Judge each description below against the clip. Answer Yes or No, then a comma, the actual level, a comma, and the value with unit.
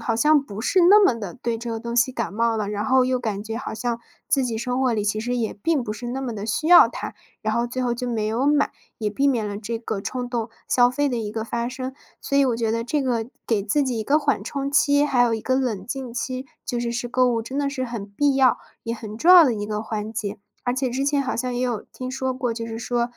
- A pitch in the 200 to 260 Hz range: Yes, high, 240 Hz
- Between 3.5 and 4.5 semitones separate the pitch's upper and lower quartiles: No, average, 2.8 semitones